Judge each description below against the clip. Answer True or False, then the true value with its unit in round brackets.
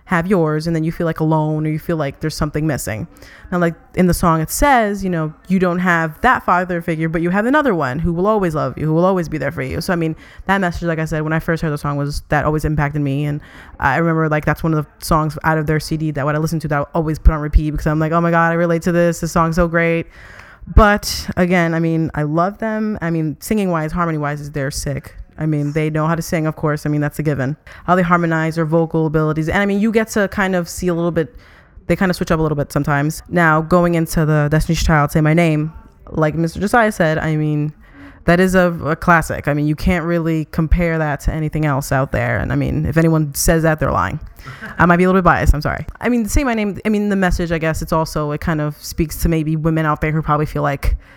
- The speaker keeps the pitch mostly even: True (2.1 semitones)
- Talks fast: True (280 wpm)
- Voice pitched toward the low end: False (160 Hz)